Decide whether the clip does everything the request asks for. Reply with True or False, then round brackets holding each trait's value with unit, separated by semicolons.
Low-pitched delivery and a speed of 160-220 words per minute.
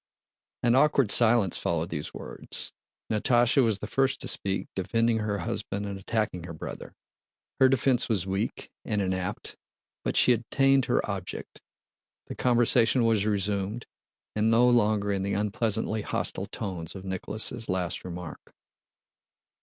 False (105 Hz; 140 wpm)